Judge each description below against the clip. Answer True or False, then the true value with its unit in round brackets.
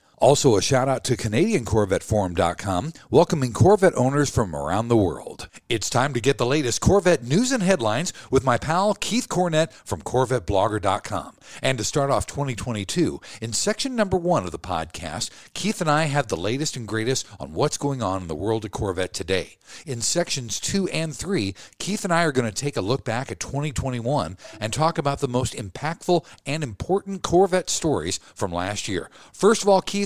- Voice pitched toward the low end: True (130 Hz)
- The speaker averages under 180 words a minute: False (190 wpm)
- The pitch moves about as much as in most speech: False (7.6 semitones)